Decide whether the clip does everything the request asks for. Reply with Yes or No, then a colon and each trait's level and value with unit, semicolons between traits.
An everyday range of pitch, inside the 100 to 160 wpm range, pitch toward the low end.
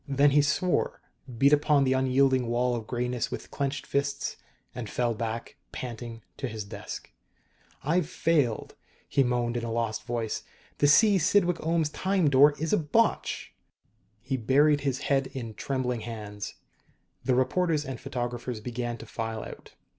Yes: average, 3.6 semitones; average, 155 wpm; low, 130 Hz